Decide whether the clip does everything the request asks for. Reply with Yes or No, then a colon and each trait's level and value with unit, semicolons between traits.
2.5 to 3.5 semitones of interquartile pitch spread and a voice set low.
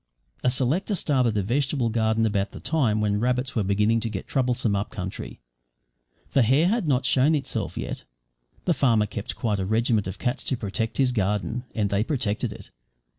No: average, 3.9 semitones; low, 115 Hz